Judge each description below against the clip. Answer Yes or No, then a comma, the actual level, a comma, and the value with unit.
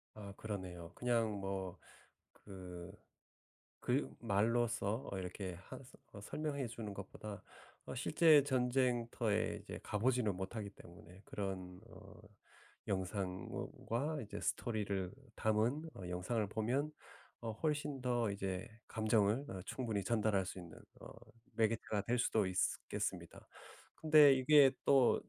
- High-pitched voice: No, low, 110 Hz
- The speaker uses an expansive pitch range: No, average, 4.2 semitones